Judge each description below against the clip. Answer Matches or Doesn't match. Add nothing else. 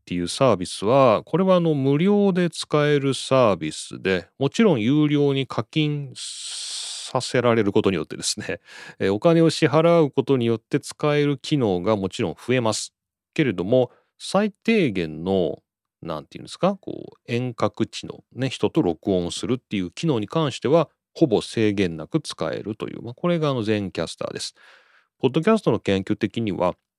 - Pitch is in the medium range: Doesn't match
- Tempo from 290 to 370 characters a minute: Matches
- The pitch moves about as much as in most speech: Doesn't match